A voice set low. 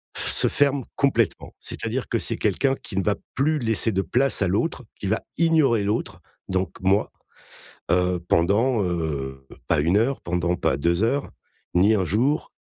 Yes: low, 105 Hz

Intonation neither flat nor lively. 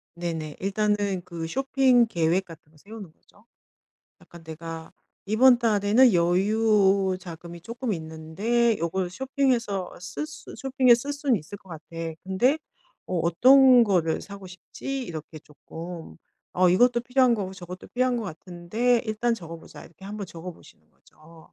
No: wide, 5.7 semitones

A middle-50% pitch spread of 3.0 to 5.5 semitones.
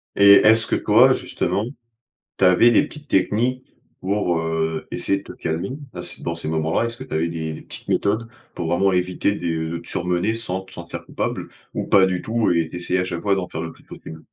Yes: average, 3.7 semitones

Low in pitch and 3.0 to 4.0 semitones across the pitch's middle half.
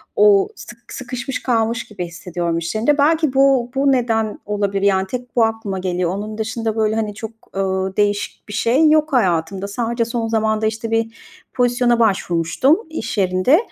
No: high, 225 Hz; average, 3.7 semitones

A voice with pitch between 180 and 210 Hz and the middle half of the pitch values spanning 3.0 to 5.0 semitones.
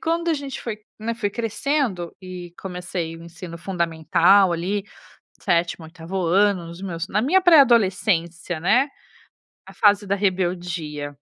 Yes: medium, 185 Hz; average, 4.2 semitones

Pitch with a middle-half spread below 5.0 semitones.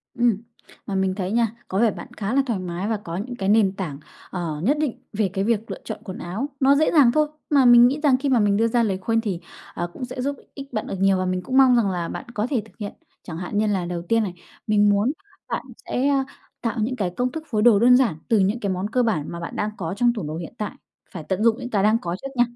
Yes: average, 4.4 semitones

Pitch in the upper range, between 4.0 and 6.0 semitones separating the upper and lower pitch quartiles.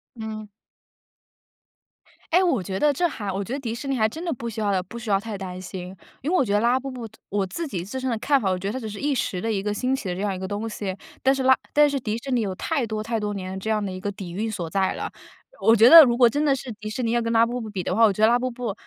Yes: high, 220 Hz; average, 4.4 semitones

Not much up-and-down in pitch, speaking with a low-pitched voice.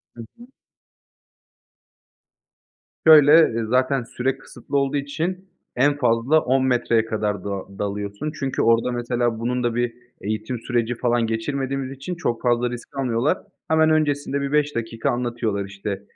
No: average, 3.3 semitones; low, 125 Hz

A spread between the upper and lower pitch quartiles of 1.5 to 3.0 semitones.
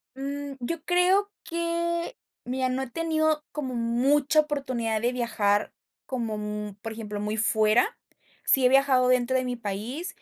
No: average, 4.9 semitones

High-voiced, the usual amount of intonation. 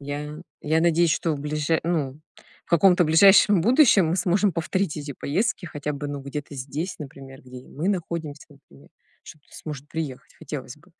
No: medium, 155 Hz; average, 3.3 semitones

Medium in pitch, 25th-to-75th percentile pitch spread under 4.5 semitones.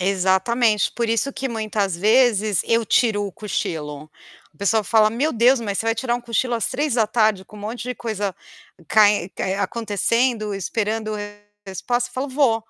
No: high, 220 Hz; average, 2.9 semitones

